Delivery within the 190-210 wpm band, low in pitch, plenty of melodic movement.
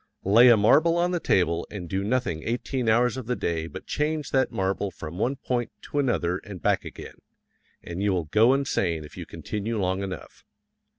Yes: average, 195 wpm; low, 105 Hz; wide, 5.8 semitones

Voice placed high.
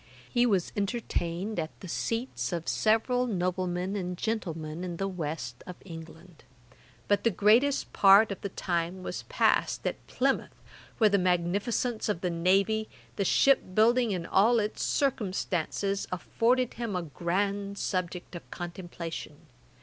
Yes: high, 195 Hz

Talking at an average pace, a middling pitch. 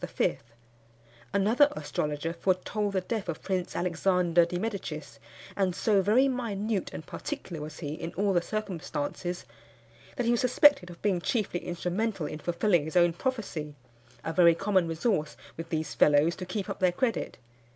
Yes: average, 160 wpm; medium, 180 Hz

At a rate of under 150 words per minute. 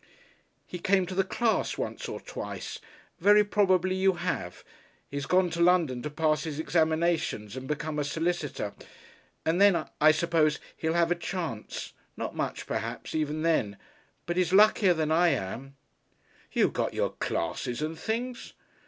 No: average, 155 wpm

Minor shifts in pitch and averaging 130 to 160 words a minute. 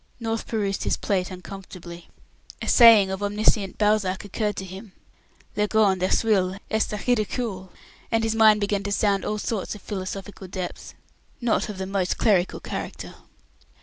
Yes: narrow, 2.3 semitones; average, 155 wpm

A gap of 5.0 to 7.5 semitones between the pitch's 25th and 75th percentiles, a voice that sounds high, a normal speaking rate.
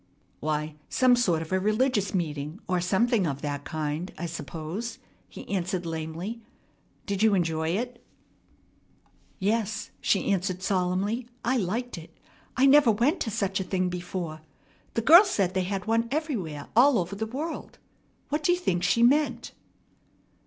Yes: wide, 5.5 semitones; high, 195 Hz; average, 155 wpm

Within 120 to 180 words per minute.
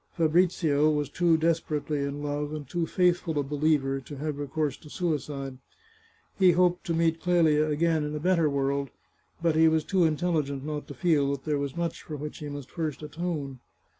No: average, 190 wpm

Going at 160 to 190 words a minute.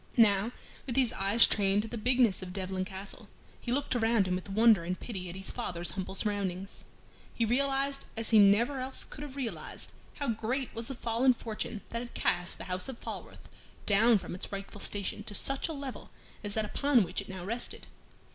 No: fast, 205 wpm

